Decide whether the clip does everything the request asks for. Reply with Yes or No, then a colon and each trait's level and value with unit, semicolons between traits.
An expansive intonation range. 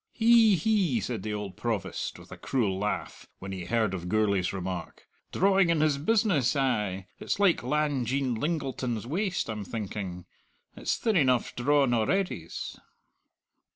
Yes: wide, 7.8 semitones